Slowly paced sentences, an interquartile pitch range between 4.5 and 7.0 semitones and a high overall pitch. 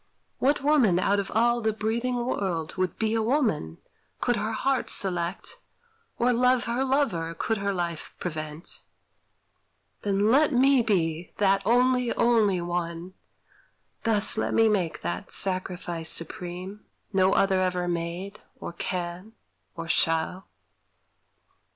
Yes: slow, 130 wpm; average, 5.1 semitones; high, 195 Hz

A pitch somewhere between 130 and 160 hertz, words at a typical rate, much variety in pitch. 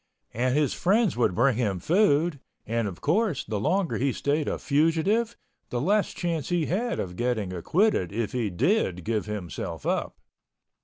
Yes: medium, 140 Hz; average, 160 wpm; wide, 8.5 semitones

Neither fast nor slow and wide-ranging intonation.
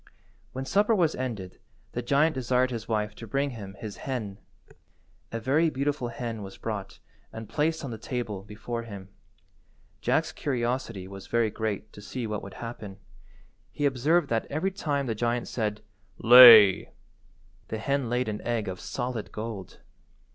No: average, 160 wpm; average, 3.8 semitones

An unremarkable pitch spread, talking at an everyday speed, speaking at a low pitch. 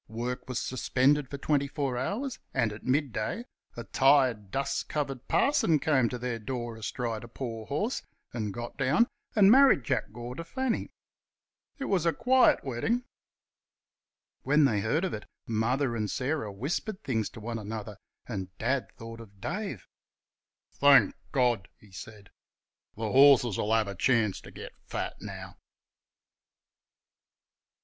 Yes: average, 4.6 semitones; average, 145 wpm; low, 125 Hz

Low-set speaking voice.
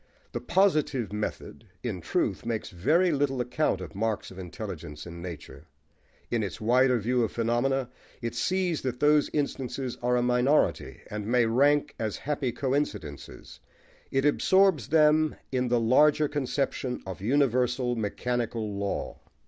Yes: low, 125 Hz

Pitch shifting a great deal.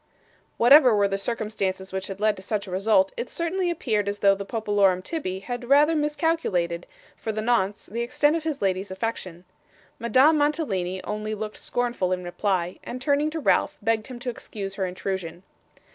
Yes: wide, 5.7 semitones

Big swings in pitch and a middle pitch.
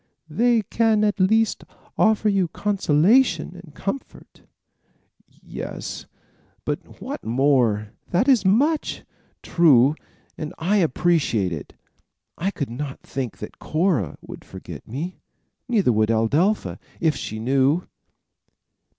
Yes: wide, 7.9 semitones; medium, 170 Hz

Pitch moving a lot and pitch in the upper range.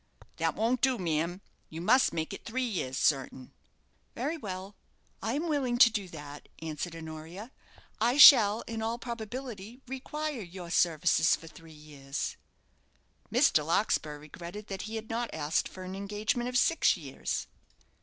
Yes: wide, 6.8 semitones; high, 200 Hz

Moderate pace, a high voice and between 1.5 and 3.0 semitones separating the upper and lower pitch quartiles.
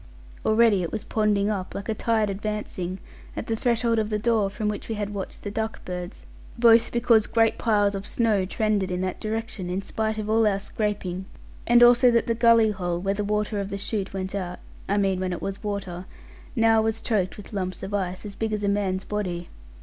No: fast, 220 wpm; high, 210 Hz; narrow, 2.5 semitones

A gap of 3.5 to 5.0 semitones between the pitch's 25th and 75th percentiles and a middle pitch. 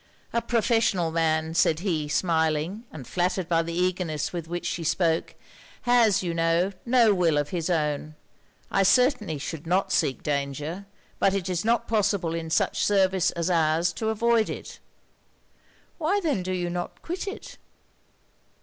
Yes: average, 3.9 semitones; medium, 175 Hz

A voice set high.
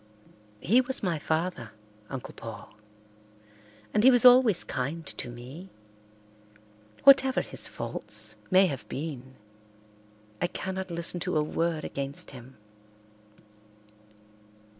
No: medium, 165 Hz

